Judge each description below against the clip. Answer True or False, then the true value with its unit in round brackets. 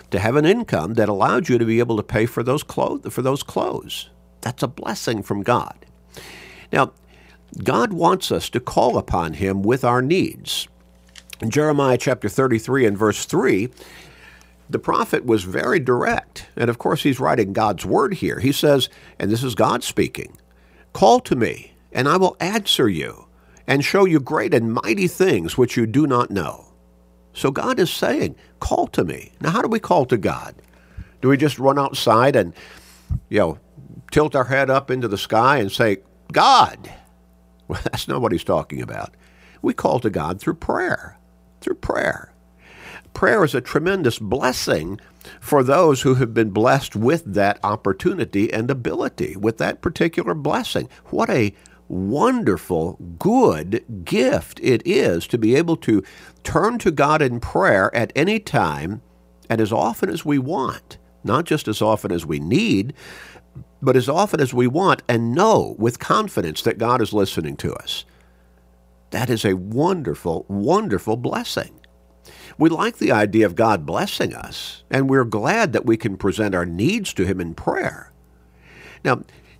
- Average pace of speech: True (170 wpm)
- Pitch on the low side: True (110 Hz)